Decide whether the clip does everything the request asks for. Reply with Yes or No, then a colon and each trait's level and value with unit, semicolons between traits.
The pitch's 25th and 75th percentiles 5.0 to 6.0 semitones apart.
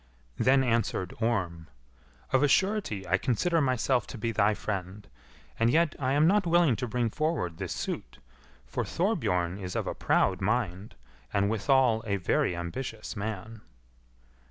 Yes: wide, 5.6 semitones